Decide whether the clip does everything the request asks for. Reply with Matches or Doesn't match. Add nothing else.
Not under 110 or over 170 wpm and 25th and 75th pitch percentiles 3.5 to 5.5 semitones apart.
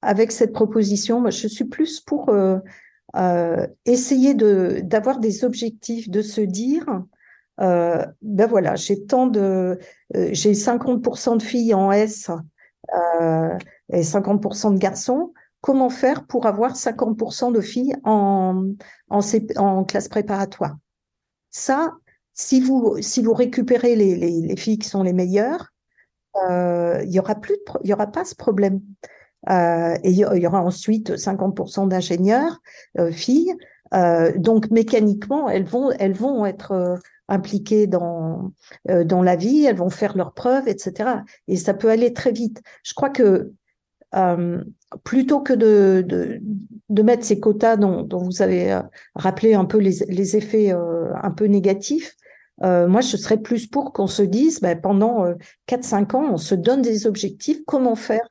Matches